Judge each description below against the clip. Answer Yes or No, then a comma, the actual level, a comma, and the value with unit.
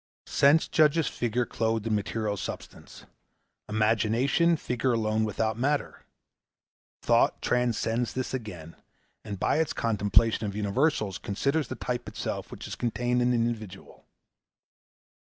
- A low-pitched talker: Yes, low, 115 Hz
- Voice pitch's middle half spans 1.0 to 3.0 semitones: Yes, narrow, 2.6 semitones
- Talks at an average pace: No, slow, 125 wpm